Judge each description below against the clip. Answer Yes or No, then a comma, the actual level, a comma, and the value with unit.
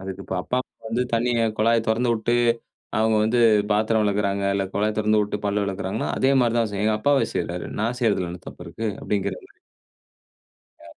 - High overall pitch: No, low, 110 Hz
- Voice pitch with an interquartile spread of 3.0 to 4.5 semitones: No, narrow, 2.5 semitones